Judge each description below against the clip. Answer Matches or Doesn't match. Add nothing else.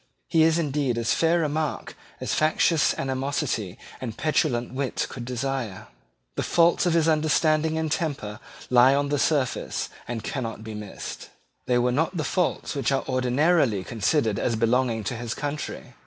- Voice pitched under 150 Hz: Matches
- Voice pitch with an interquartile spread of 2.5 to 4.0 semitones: Doesn't match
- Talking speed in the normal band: Matches